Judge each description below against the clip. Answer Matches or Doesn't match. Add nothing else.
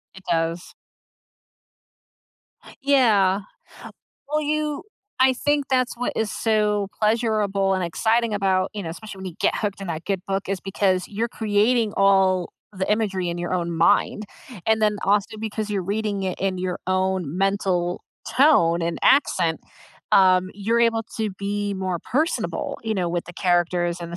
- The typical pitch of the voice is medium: Doesn't match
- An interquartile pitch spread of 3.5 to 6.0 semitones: Doesn't match